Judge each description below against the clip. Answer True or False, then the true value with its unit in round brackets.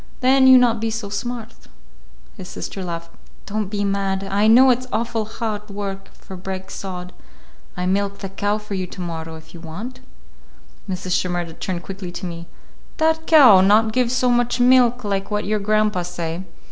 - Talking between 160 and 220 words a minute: True (180 wpm)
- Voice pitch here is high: True (200 Hz)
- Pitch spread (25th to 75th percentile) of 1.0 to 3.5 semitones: False (3.9 semitones)